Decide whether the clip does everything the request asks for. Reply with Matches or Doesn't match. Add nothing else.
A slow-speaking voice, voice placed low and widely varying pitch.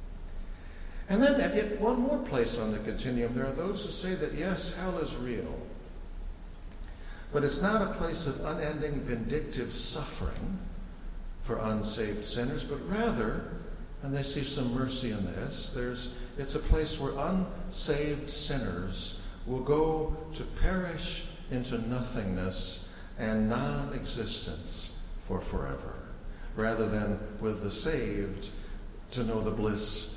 Matches